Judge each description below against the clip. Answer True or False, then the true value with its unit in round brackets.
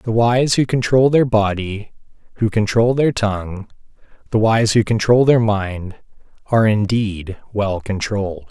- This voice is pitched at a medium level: False (110 Hz)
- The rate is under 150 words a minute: True (140 wpm)